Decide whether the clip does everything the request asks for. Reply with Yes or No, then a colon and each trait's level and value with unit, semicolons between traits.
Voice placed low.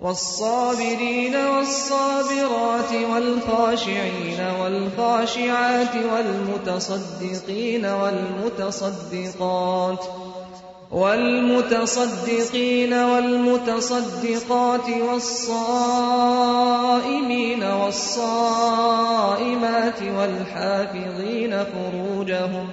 No: high, 230 Hz